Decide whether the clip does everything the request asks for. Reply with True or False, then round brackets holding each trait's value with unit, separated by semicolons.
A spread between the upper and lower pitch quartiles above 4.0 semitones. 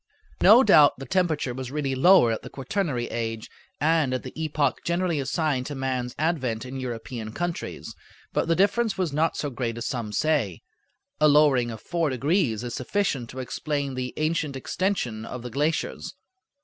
True (4.7 semitones)